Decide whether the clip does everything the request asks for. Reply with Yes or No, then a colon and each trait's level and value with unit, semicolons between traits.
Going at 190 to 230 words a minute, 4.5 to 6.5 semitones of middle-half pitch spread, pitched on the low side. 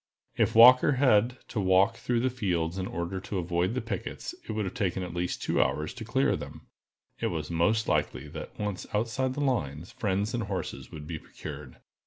Yes: average, 195 wpm; average, 5.1 semitones; low, 100 Hz